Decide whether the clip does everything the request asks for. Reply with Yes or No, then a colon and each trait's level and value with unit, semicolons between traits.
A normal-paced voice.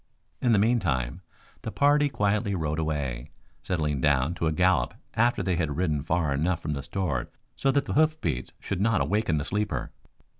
Yes: average, 180 wpm